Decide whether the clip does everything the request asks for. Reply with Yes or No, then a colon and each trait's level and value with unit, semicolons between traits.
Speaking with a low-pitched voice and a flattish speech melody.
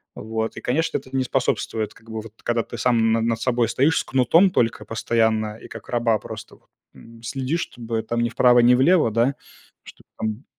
Yes: low, 115 Hz; narrow, 2.3 semitones